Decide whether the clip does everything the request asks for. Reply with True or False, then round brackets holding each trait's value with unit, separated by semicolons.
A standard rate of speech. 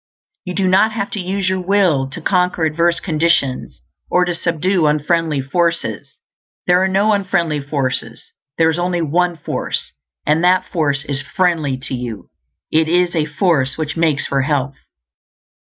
True (160 wpm)